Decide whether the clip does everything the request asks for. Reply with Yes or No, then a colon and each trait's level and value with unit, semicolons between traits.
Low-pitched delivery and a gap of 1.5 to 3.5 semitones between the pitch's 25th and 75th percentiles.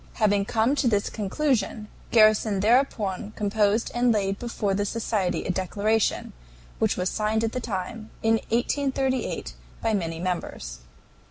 No: high, 215 Hz; narrow, 2.6 semitones